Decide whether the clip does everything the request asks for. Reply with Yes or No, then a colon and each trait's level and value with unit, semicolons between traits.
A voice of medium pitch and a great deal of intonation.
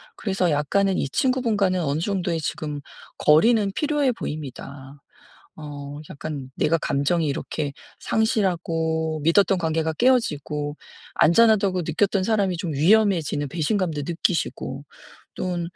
No: medium, 170 Hz; average, 4.9 semitones